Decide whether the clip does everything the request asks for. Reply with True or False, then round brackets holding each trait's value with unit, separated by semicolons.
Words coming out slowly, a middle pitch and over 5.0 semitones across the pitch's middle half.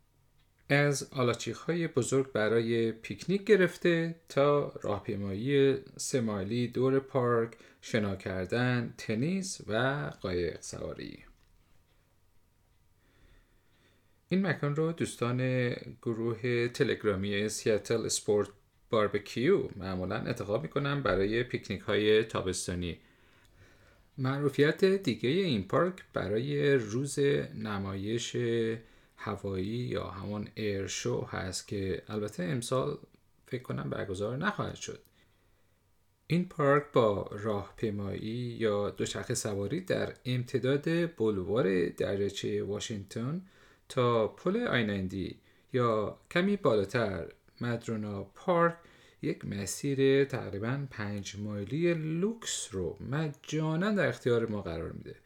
False (95 wpm; 115 Hz; 5.6 semitones)